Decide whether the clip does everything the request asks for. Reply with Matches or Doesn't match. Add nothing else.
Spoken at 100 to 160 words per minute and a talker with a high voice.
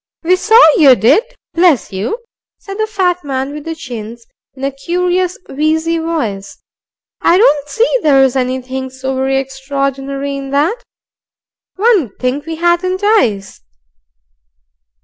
Matches